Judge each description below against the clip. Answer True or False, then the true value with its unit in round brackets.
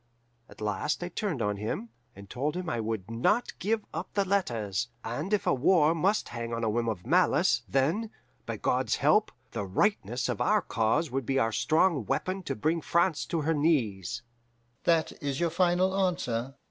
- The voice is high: False (140 Hz)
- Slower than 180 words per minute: False (185 wpm)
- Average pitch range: False (7.6 semitones)